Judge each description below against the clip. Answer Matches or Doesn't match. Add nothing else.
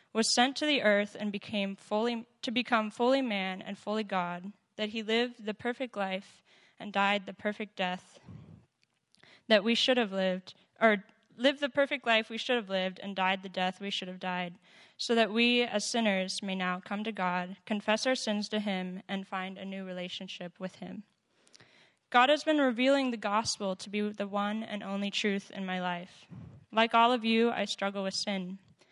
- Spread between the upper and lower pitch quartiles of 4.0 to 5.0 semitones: Doesn't match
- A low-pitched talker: Doesn't match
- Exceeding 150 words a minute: Matches